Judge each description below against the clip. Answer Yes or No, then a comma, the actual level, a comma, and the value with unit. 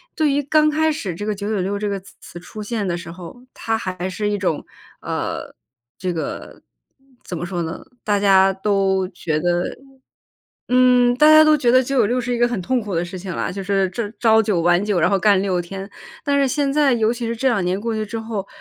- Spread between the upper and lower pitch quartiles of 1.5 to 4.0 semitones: No, average, 4.7 semitones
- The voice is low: No, high, 205 Hz